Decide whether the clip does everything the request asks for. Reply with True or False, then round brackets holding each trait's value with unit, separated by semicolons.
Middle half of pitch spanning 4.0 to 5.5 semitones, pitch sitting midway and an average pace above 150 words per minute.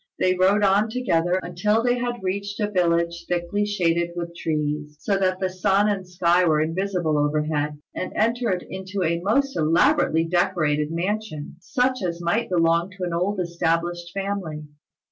False (3.2 semitones; 180 Hz; 160 wpm)